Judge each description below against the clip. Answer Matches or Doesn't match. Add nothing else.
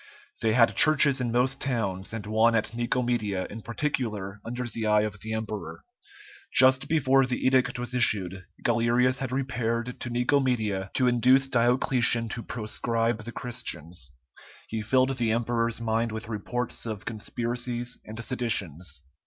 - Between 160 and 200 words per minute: Doesn't match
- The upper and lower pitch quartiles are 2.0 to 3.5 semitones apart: Matches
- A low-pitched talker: Matches